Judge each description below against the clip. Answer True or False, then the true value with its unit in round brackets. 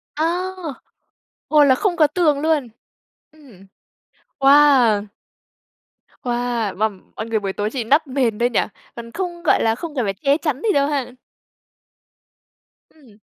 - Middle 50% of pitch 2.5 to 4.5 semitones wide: False (5.1 semitones)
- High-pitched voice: True (270 Hz)